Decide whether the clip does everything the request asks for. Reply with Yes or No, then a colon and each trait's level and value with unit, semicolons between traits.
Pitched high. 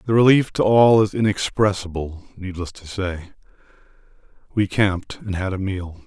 No: low, 100 Hz